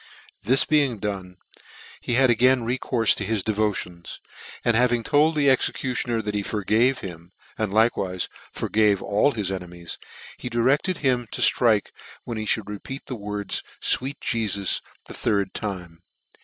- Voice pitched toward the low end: Yes, low, 110 Hz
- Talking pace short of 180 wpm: Yes, average, 160 wpm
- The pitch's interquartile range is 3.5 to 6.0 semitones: Yes, average, 3.8 semitones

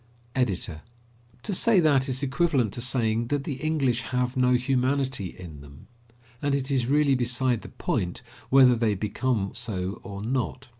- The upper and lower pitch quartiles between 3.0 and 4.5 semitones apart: Yes, average, 3.4 semitones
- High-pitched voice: No, low, 125 Hz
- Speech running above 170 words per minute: No, average, 160 wpm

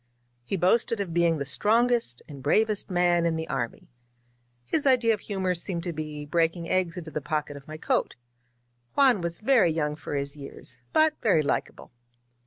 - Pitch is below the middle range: No, medium, 170 Hz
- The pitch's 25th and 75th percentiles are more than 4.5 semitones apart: Yes, average, 5.3 semitones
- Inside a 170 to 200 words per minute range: Yes, average, 180 wpm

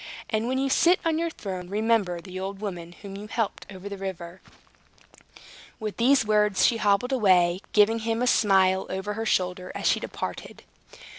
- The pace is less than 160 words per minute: No, average, 175 wpm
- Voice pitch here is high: Yes, high, 205 Hz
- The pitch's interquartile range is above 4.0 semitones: No, average, 3.3 semitones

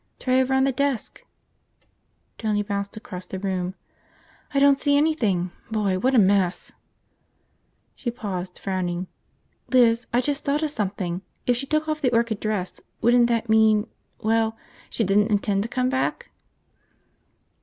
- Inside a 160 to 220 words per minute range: No, average, 150 wpm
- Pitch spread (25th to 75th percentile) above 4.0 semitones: Yes, average, 4.5 semitones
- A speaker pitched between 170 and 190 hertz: No, high, 220 Hz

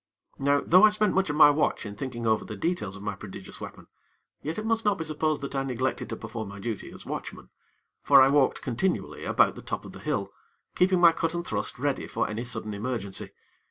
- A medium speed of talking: No, fast, 230 wpm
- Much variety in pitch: Yes, wide, 7.1 semitones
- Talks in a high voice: No, low, 135 Hz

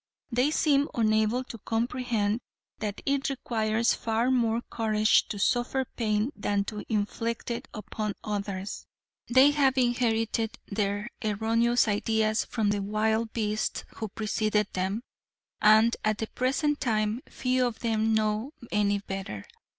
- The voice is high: Yes, high, 220 Hz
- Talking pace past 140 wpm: No, slow, 135 wpm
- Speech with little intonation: Yes, narrow, 2.3 semitones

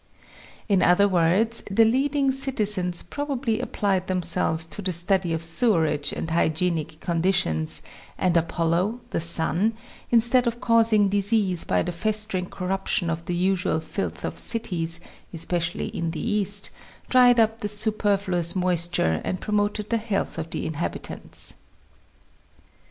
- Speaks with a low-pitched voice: No, medium, 185 Hz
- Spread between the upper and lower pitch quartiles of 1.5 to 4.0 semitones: No, average, 4.4 semitones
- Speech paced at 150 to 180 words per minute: No, average, 140 wpm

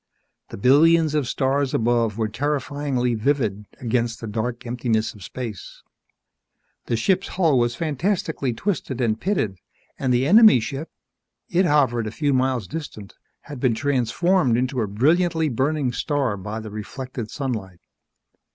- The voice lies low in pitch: Yes, low, 130 Hz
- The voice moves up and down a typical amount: Yes, average, 4.4 semitones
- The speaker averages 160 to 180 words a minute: No, average, 140 wpm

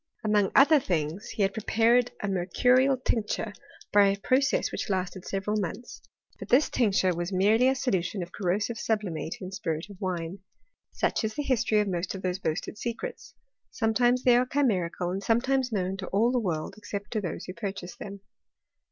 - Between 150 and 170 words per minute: No, average, 185 wpm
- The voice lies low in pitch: No, high, 205 Hz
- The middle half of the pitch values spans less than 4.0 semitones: No, average, 4.5 semitones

